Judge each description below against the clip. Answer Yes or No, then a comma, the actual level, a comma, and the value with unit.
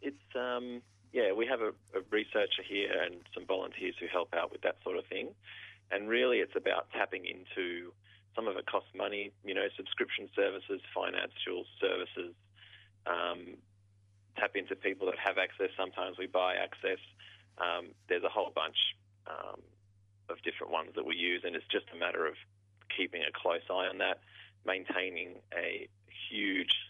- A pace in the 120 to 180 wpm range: Yes, average, 165 wpm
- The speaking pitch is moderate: No, low, 100 Hz